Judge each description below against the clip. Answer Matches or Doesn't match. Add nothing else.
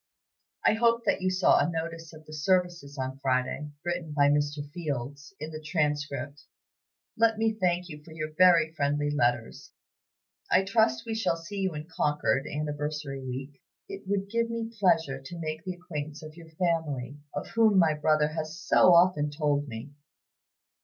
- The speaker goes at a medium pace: Matches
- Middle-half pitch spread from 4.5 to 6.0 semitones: Doesn't match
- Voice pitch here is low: Doesn't match